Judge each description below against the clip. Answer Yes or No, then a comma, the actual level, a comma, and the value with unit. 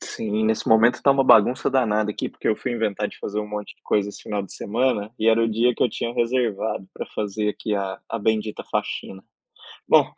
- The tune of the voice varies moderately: No, narrow, 2.0 semitones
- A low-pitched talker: Yes, low, 110 Hz